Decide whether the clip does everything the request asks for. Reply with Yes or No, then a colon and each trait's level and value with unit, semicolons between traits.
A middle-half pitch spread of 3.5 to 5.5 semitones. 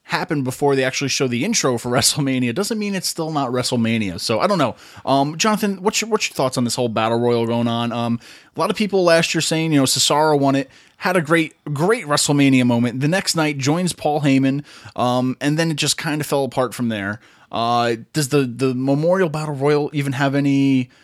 Yes: average, 4.2 semitones